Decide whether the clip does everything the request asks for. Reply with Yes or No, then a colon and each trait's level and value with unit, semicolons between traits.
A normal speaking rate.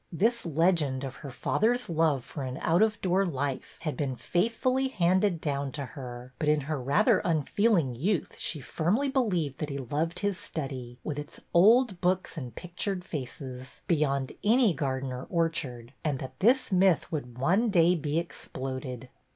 Yes: average, 165 wpm